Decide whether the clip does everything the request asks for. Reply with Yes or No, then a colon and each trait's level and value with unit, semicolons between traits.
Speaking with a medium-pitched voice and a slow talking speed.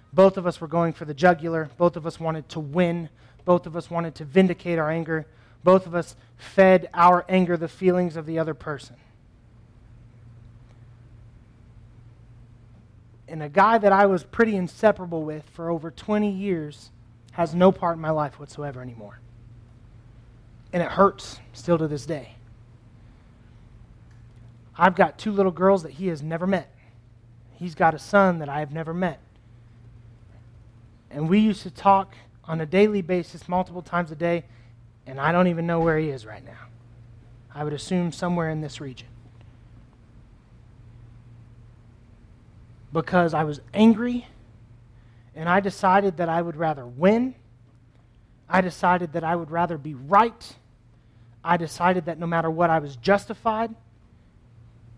No: medium, 150 Hz; average, 155 wpm